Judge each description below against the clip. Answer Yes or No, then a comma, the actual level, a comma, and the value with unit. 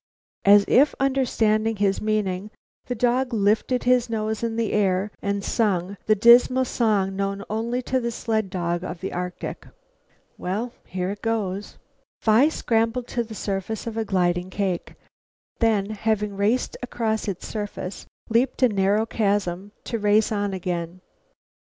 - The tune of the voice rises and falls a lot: No, average, 2.8 semitones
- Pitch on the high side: Yes, high, 215 Hz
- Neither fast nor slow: Yes, average, 145 wpm